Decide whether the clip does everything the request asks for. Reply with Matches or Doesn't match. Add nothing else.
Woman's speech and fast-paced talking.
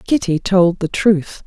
Doesn't match